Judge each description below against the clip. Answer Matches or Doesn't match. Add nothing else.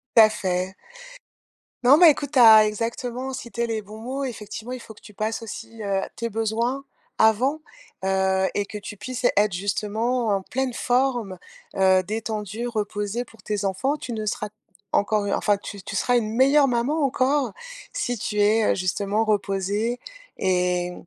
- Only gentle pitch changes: Doesn't match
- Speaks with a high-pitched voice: Matches